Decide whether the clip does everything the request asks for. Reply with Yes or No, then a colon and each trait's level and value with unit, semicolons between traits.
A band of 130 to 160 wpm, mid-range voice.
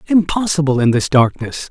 Yes: average, 140 wpm; medium, 150 Hz